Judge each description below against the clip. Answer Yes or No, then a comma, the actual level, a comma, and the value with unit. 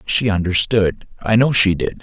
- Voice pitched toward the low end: Yes, low, 100 Hz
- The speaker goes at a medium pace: Yes, average, 180 wpm